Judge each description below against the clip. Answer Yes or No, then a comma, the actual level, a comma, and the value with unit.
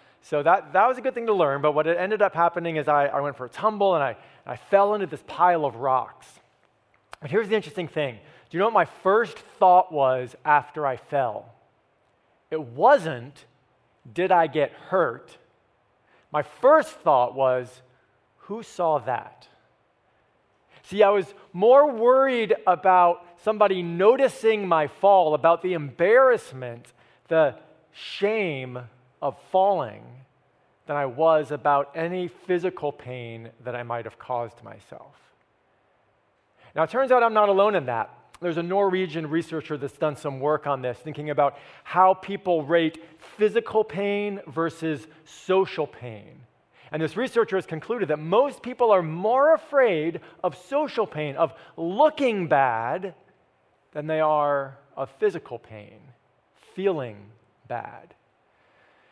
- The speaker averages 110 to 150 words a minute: Yes, average, 145 wpm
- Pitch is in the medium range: Yes, medium, 160 Hz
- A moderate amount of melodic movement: No, wide, 5.9 semitones